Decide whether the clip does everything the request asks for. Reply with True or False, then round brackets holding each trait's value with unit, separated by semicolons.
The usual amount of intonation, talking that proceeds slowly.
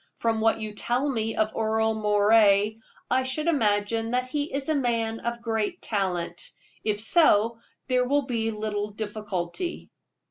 False (3.0 semitones; 150 wpm)